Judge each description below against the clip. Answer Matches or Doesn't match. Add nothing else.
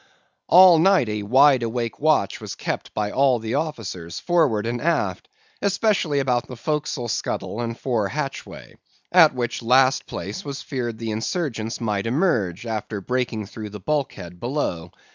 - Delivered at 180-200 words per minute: Doesn't match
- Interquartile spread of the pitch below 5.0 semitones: Doesn't match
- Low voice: Matches